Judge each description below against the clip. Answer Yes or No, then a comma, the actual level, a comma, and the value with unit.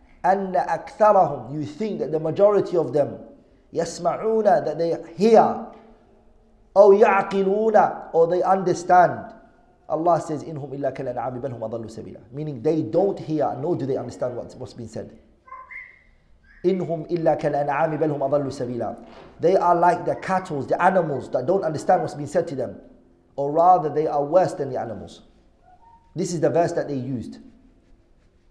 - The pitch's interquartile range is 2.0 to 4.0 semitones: No, average, 4.4 semitones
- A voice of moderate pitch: Yes, medium, 165 Hz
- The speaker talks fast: No, average, 160 wpm